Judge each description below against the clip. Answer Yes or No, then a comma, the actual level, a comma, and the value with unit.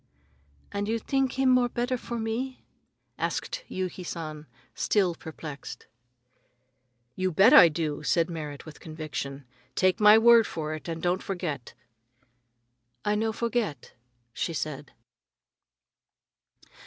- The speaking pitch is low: No, medium, 185 Hz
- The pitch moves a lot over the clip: Yes, wide, 6.5 semitones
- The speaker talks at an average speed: No, slow, 120 wpm